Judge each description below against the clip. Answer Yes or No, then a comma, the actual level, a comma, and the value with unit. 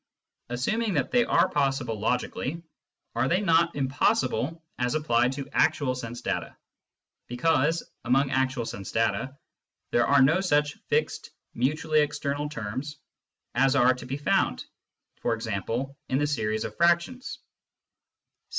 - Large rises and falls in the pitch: No, average, 3.7 semitones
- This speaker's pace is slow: Yes, slow, 130 wpm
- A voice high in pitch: No, low, 135 Hz